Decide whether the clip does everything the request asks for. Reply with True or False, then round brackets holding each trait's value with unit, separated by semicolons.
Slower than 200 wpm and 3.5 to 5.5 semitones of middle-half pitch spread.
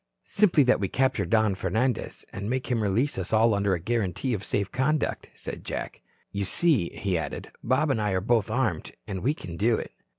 False (205 wpm; 4.9 semitones)